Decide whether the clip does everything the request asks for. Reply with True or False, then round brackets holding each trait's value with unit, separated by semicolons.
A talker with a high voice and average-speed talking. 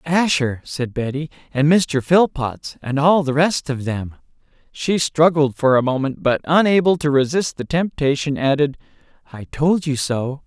False (145 Hz; 160 wpm)